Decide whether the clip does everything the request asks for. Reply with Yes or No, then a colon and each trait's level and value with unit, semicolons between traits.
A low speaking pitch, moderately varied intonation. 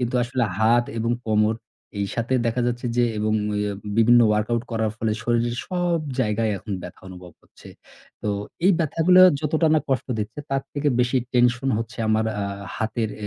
Yes: low, 120 Hz; average, 3.0 semitones